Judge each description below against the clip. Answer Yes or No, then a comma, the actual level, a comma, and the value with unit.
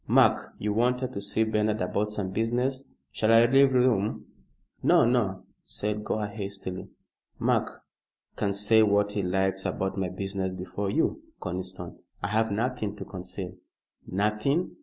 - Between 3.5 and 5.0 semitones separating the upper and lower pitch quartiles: No, average, 2.8 semitones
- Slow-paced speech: No, average, 150 wpm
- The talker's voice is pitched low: Yes, low, 105 Hz